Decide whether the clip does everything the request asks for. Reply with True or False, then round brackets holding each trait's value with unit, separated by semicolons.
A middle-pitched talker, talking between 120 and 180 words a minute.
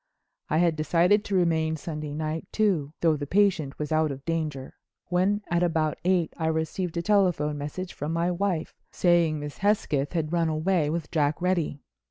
True (165 Hz; 170 wpm)